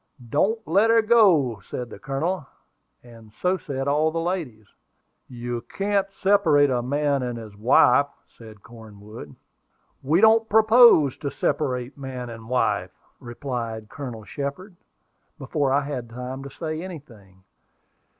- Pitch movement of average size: No, wide, 6.0 semitones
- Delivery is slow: Yes, slow, 130 wpm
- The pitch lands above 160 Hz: No, medium, 140 Hz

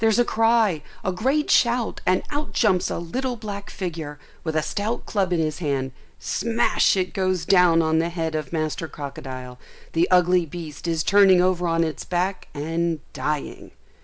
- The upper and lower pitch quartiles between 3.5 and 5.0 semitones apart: Yes, average, 4.1 semitones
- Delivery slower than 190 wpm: Yes, average, 175 wpm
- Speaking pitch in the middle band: Yes, medium, 175 Hz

